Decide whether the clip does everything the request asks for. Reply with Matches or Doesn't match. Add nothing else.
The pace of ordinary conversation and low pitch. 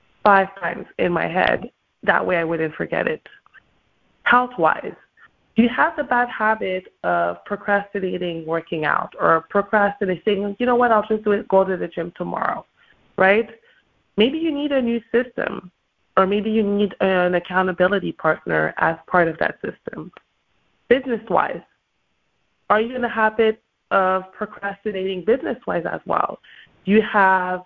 Doesn't match